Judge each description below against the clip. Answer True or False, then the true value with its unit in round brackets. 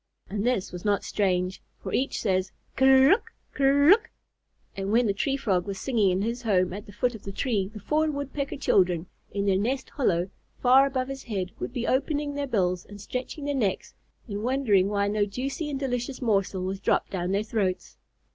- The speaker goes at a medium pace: False (210 wpm)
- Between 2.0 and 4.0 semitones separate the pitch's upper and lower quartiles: False (5.6 semitones)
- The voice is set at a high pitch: True (215 Hz)